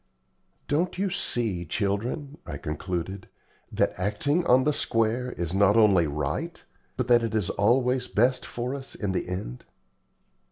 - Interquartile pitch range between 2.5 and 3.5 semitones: No, average, 5.2 semitones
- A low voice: Yes, low, 110 Hz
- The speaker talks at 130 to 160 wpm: Yes, average, 150 wpm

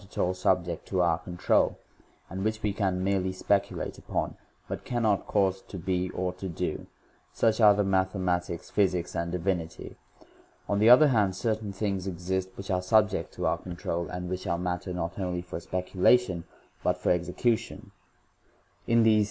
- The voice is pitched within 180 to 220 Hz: No, very low, 95 Hz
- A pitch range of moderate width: No, narrow, 2.2 semitones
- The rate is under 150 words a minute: No, average, 180 wpm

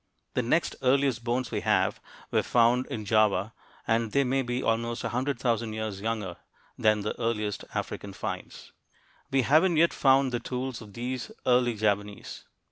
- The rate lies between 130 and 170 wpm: Yes, average, 165 wpm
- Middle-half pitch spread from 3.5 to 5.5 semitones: No, average, 3.0 semitones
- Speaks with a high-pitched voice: No, low, 120 Hz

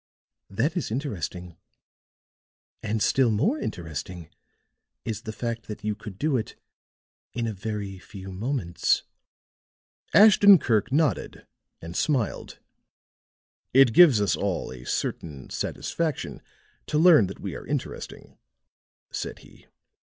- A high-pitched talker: No, low, 110 Hz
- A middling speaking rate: No, slow, 120 wpm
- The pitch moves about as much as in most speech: No, wide, 6.5 semitones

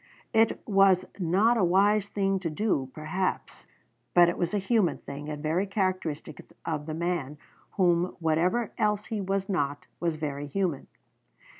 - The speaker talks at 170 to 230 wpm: No, average, 155 wpm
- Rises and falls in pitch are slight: No, average, 4.0 semitones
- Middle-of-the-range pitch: Yes, medium, 180 Hz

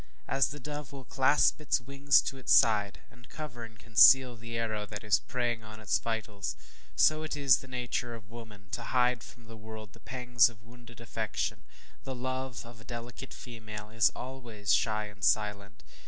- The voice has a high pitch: No, low, 115 Hz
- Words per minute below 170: No, average, 185 wpm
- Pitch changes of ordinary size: Yes, average, 3.0 semitones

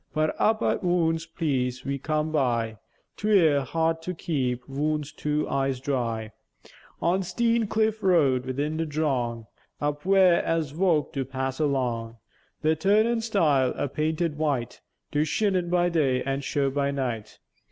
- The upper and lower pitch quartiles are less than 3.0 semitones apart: No, average, 4.3 semitones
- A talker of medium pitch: Yes, medium, 150 Hz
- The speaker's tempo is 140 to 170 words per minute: Yes, average, 150 wpm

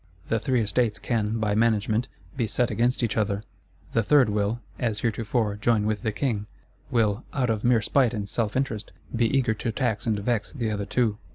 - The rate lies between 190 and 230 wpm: Yes, average, 195 wpm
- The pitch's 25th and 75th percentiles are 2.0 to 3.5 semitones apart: Yes, narrow, 2.4 semitones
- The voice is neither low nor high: No, low, 110 Hz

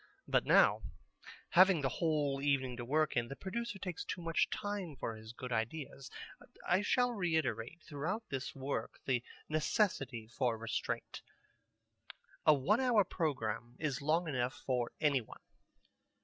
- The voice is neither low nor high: Yes, medium, 145 Hz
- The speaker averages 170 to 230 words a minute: No, average, 145 wpm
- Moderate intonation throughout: No, wide, 5.7 semitones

